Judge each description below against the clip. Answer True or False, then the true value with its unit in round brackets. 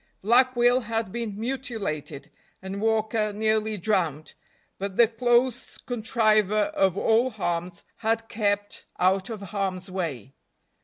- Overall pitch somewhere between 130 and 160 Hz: False (215 Hz)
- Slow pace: True (120 wpm)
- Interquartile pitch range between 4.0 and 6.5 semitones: False (3.2 semitones)